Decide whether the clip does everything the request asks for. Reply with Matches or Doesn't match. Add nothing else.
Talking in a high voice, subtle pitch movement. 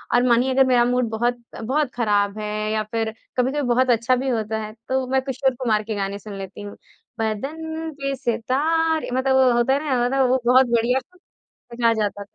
Doesn't match